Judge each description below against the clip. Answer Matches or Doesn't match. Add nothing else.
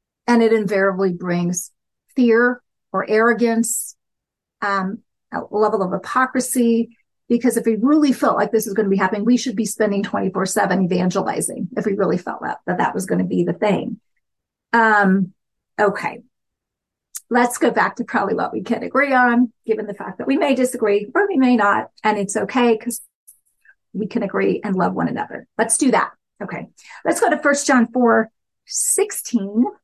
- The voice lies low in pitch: Doesn't match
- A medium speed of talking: Matches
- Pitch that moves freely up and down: Doesn't match